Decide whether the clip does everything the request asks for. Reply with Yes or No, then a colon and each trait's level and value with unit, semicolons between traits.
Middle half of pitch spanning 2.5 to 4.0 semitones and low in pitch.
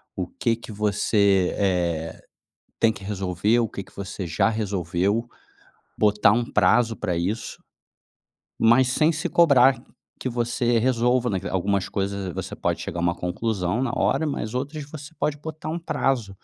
No: average, 4.4 semitones; low, 110 Hz